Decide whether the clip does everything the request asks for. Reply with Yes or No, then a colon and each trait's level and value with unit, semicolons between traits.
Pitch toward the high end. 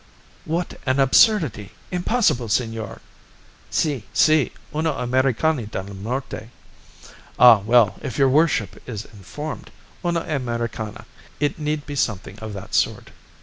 No: low, 125 Hz